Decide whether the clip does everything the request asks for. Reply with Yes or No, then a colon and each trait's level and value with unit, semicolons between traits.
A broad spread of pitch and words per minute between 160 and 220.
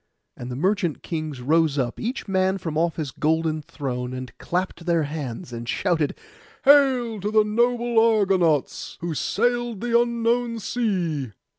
No: wide, 7.3 semitones; average, 150 wpm